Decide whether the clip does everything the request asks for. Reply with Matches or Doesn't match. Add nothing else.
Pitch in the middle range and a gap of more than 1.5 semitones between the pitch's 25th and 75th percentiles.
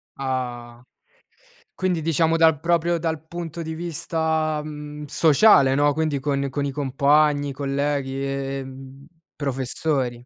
Matches